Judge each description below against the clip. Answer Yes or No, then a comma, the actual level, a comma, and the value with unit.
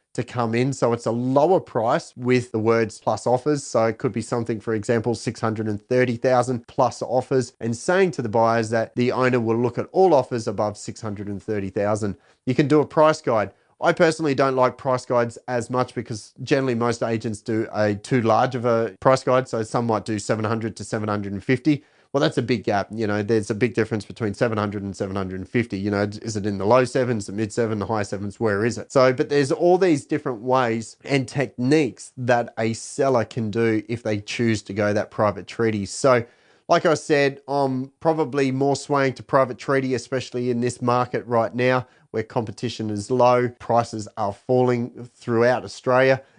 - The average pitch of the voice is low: Yes, low, 120 Hz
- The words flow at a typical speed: Yes, average, 195 wpm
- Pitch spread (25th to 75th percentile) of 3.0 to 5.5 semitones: No, narrow, 2.6 semitones